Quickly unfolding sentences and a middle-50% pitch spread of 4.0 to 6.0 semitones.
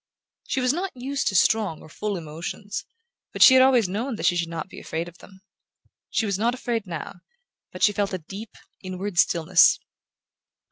No: average, 190 wpm; average, 5.2 semitones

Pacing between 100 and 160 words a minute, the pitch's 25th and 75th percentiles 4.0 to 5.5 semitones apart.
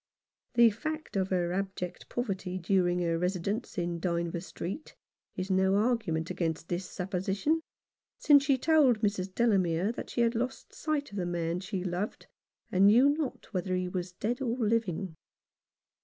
Yes: average, 155 wpm; average, 4.9 semitones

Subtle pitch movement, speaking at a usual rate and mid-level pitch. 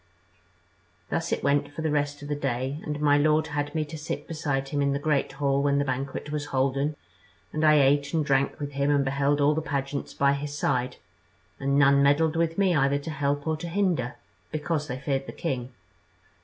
No: narrow, 1.6 semitones; fast, 210 wpm; medium, 145 Hz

